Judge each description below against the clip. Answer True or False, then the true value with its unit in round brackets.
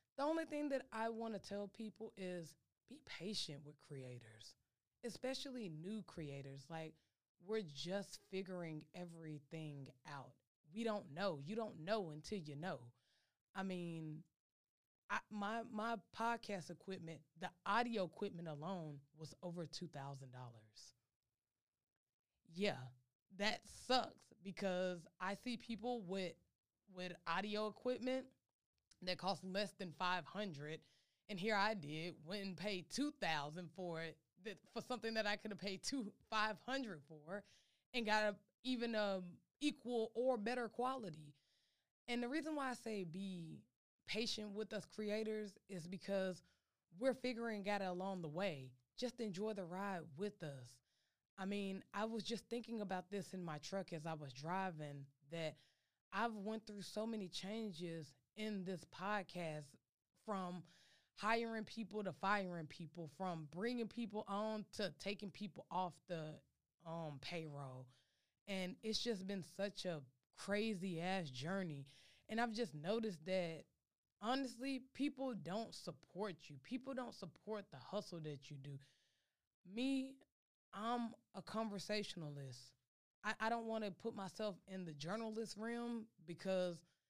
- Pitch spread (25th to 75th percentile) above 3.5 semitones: True (5.2 semitones)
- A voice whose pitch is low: False (190 Hz)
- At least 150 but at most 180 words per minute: False (140 wpm)